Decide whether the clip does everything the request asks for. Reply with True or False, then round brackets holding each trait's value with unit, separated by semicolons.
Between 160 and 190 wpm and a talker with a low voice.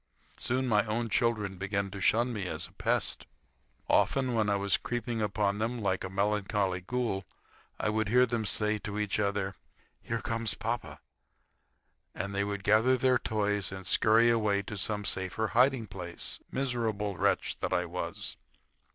True (165 wpm; 105 Hz)